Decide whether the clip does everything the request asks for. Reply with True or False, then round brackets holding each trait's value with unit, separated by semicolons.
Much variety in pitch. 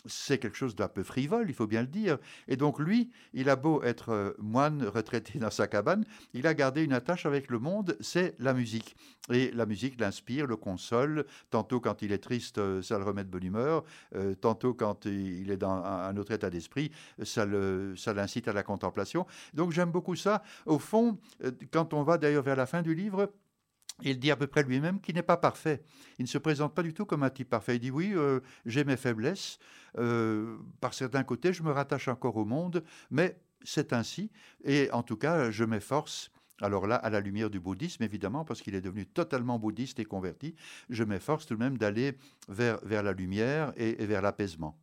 True (6.1 semitones)